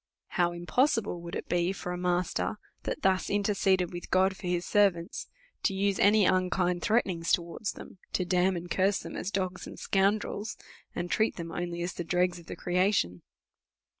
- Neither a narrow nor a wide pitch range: No, narrow, 2.0 semitones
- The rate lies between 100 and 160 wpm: No, average, 190 wpm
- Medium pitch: Yes, medium, 180 Hz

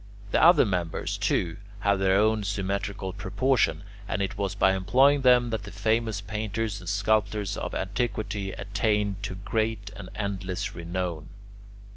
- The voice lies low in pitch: Yes, low, 100 Hz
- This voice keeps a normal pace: Yes, average, 145 wpm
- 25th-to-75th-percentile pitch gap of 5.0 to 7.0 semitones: No, narrow, 2.4 semitones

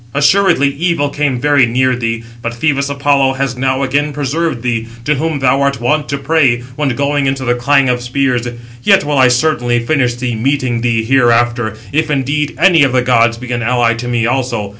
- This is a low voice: Yes, low, 130 Hz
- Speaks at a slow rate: No, average, 200 wpm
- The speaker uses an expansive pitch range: No, average, 2.9 semitones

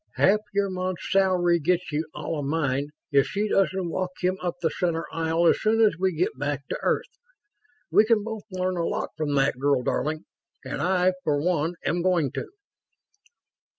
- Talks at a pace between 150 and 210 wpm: Yes, average, 185 wpm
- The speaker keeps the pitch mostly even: No, average, 3.4 semitones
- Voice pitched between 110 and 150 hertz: No, medium, 175 Hz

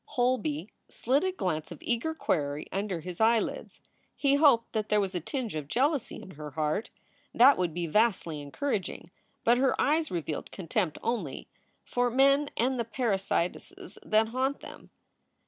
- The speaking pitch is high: Yes, high, 220 Hz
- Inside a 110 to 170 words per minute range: Yes, average, 160 wpm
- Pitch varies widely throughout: Yes, wide, 7.4 semitones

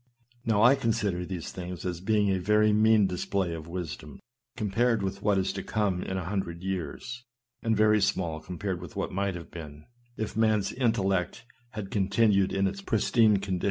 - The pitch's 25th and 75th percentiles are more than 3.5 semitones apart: No, average, 3.1 semitones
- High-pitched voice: No, low, 100 Hz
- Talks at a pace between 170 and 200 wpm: Yes, average, 180 wpm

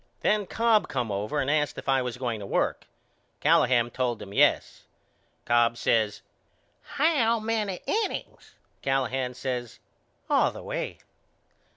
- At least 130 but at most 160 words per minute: Yes, slow, 135 wpm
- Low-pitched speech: Yes, low, 130 Hz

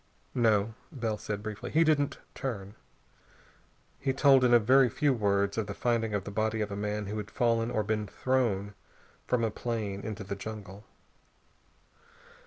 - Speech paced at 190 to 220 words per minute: No, average, 170 wpm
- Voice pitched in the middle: No, low, 110 Hz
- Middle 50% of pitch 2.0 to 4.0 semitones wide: Yes, average, 3.0 semitones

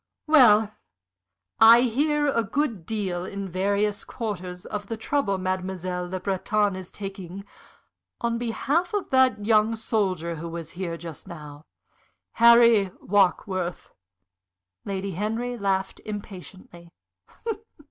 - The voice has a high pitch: Yes, high, 200 Hz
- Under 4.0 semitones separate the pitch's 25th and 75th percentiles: Yes, average, 3.6 semitones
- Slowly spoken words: Yes, slow, 115 wpm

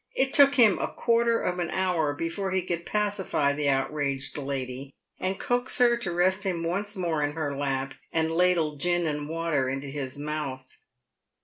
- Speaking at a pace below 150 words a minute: No, average, 180 wpm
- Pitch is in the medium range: Yes, medium, 165 Hz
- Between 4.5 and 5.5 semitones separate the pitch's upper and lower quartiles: Yes, average, 4.8 semitones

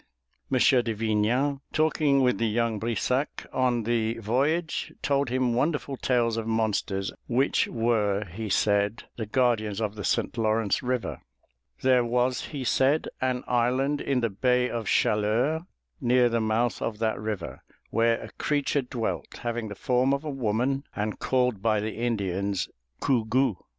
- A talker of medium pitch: No, low, 120 Hz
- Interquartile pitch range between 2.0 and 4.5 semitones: Yes, average, 3.0 semitones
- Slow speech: No, average, 155 wpm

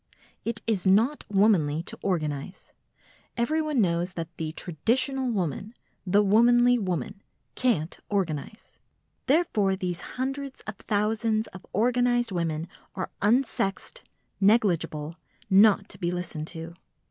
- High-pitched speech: Yes, high, 200 Hz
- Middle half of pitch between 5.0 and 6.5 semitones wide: Yes, wide, 5.5 semitones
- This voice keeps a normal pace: No, slow, 115 wpm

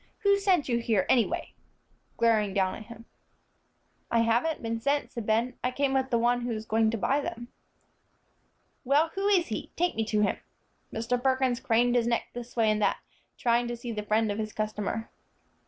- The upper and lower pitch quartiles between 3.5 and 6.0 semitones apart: No, average, 2.7 semitones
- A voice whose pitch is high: Yes, high, 235 Hz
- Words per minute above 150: Yes, average, 195 wpm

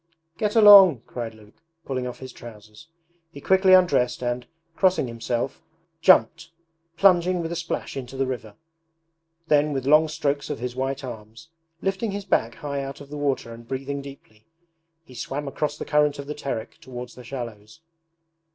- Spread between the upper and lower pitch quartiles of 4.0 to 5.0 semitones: Yes, average, 4.7 semitones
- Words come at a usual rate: Yes, average, 170 wpm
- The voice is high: No, low, 135 Hz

